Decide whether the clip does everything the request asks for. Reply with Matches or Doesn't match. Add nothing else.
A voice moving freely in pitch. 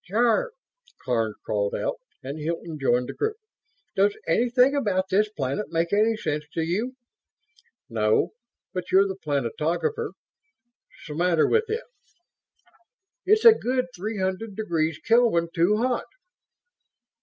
Matches